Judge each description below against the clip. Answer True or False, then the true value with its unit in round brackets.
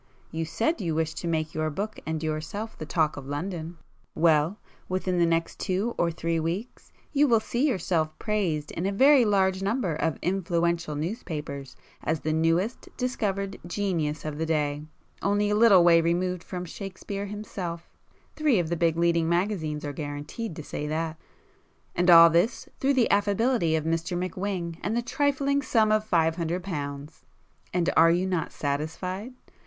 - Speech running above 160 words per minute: True (170 wpm)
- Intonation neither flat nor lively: True (4.2 semitones)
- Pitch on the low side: False (170 Hz)